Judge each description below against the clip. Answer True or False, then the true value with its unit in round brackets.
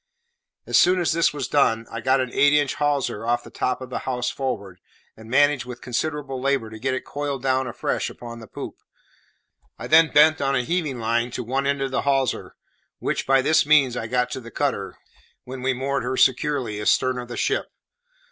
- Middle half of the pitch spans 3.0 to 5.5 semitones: False (2.6 semitones)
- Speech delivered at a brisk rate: True (210 wpm)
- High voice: False (130 Hz)